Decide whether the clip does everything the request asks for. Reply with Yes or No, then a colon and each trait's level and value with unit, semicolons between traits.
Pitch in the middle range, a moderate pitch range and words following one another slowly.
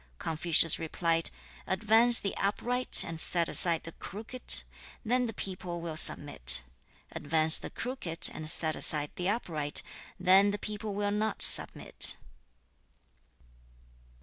Yes: medium, 180 Hz; average, 4.7 semitones; slow, 120 wpm